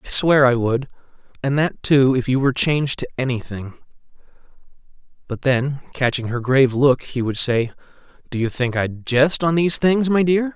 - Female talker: No, male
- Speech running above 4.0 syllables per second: Yes, 5.2 syllables/s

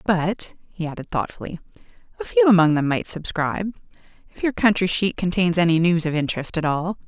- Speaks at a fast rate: No, average, 180 wpm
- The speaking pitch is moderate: Yes, medium, 175 Hz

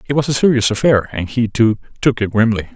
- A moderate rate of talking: No, fast, 240 wpm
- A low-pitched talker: Yes, low, 115 Hz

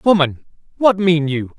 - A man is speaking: Yes, male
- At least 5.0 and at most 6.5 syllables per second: No, 4.1 syllables/s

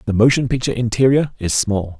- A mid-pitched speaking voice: No, low, 115 Hz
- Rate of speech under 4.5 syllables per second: No, 6.1 syllables/s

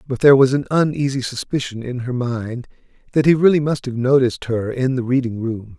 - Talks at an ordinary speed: No, fast, 210 wpm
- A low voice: Yes, low, 130 Hz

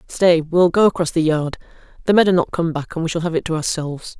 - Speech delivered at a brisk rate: Yes, fast, 270 wpm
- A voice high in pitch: No, medium, 165 Hz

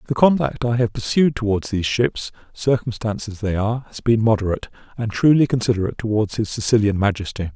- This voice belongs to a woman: No, male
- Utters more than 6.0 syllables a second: Yes, 6.3 syllables/s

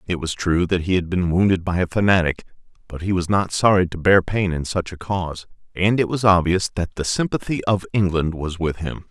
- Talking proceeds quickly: Yes, fast, 230 wpm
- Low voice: Yes, very low, 90 Hz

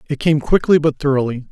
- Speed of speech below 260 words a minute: Yes, average, 200 wpm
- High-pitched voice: No, medium, 145 Hz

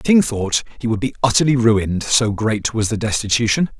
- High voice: No, low, 115 Hz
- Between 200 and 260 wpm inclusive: Yes, fast, 205 wpm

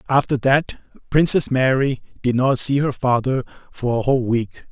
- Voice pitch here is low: Yes, low, 130 Hz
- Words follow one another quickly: No, average, 165 wpm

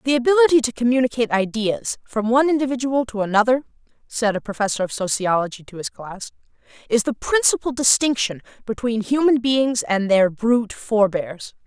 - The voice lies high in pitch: Yes, high, 230 Hz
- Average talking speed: Yes, average, 150 wpm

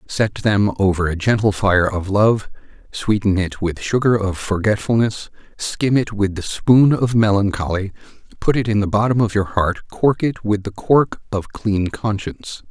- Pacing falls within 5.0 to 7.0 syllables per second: No, 4.5 syllables/s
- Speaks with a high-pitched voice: No, low, 105 Hz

